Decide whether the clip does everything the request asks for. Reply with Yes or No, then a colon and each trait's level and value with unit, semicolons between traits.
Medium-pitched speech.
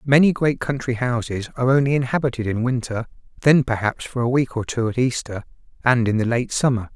No: low, 125 Hz